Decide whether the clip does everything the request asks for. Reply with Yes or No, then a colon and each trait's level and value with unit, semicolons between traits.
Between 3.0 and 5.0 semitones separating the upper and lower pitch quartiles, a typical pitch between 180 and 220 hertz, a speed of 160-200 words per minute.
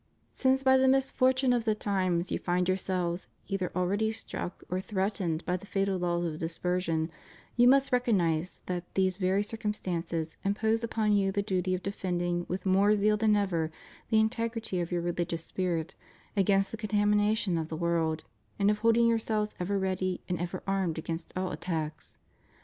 Yes: average, 3.4 semitones; high, 190 Hz; average, 170 wpm